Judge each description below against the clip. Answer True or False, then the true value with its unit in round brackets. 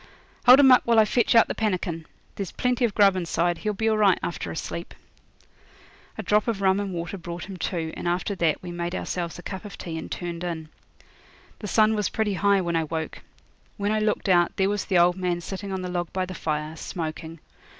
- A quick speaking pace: True (230 wpm)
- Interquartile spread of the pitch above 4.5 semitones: False (3.2 semitones)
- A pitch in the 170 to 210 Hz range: True (185 Hz)